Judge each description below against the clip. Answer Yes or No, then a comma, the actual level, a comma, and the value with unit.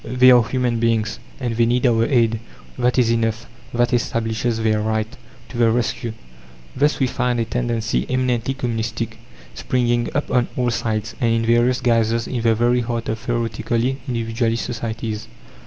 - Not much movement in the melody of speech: Yes, narrow, 1.4 semitones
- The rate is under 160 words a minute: No, average, 165 wpm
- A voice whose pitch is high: No, low, 115 Hz